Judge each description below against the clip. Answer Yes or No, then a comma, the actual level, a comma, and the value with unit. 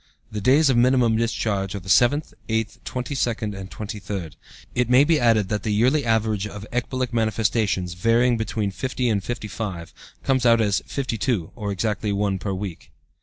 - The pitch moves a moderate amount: Yes, average, 3.3 semitones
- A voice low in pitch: Yes, low, 110 Hz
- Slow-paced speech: No, average, 175 wpm